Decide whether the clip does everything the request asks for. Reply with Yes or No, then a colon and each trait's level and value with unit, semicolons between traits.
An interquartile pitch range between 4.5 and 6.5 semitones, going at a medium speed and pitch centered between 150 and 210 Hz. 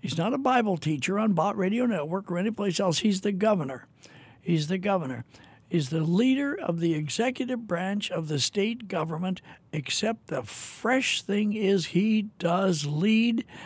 Yes: average, 4.9 semitones; average, 165 wpm; high, 190 Hz